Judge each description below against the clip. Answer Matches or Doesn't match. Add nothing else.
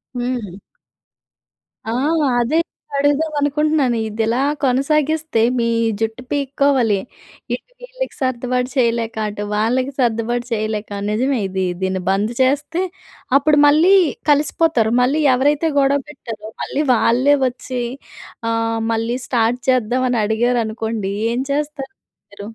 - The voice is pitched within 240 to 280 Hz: Matches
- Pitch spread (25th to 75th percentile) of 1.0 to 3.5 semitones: Doesn't match